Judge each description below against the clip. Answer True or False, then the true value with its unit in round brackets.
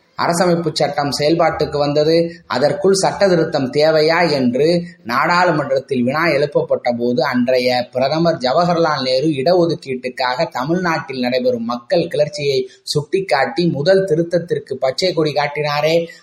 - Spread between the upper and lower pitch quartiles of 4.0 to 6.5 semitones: True (4.4 semitones)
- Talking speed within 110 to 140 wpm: False (95 wpm)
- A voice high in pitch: False (155 Hz)